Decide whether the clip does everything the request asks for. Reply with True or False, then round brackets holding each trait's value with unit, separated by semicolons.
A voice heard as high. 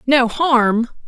True (250 Hz)